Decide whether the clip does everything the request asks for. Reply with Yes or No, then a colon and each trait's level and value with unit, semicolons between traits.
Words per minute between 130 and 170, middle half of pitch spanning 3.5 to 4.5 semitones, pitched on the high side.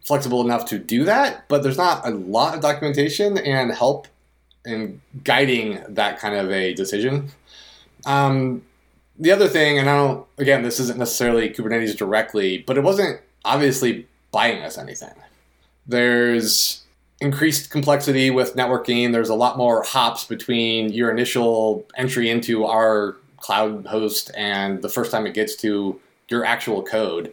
No: average, 150 wpm; average, 4.2 semitones; low, 120 Hz